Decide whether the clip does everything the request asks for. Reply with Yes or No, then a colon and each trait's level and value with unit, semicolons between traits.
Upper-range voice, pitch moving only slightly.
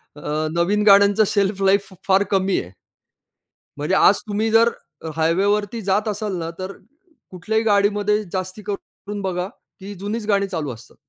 Yes: high, 200 Hz; narrow, 1.9 semitones